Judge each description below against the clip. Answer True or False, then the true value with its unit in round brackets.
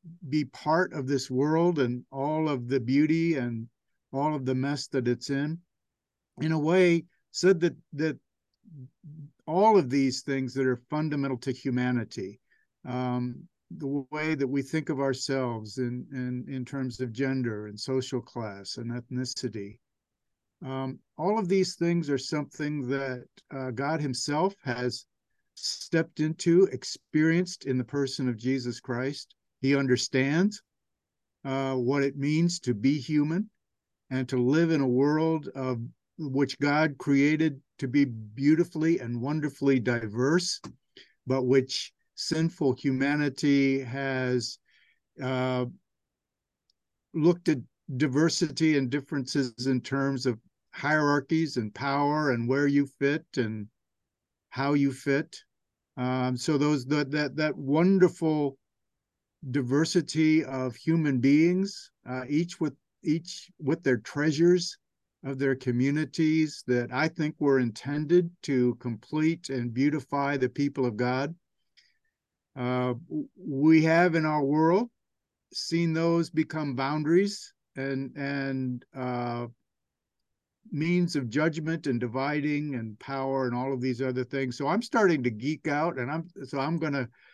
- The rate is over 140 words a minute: False (135 wpm)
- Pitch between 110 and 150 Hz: True (140 Hz)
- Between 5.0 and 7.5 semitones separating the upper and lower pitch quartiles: False (3.5 semitones)